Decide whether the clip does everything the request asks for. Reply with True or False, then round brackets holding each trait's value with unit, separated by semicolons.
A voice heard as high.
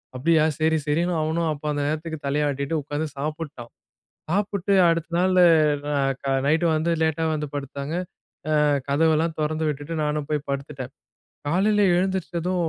False (155 Hz)